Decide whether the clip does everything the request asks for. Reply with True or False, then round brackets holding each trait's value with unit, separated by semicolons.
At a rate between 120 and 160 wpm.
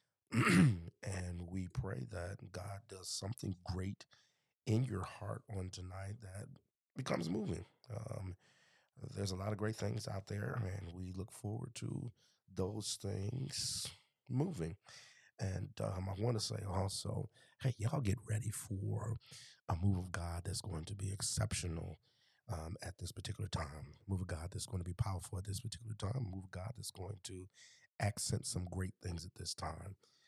False (170 wpm)